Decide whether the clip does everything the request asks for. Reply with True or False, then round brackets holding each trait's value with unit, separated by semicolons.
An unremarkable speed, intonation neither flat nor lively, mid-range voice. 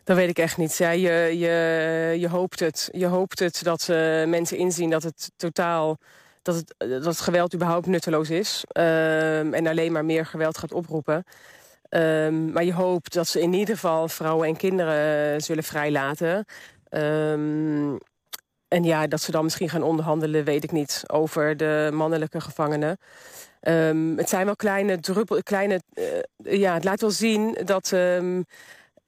False (170 wpm; 2.3 semitones; 165 Hz)